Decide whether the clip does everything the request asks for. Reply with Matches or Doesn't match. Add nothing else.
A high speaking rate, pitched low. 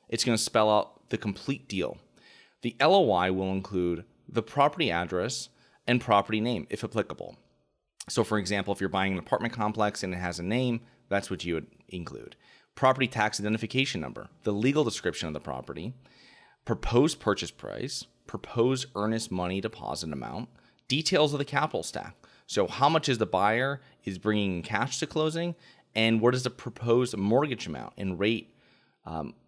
Doesn't match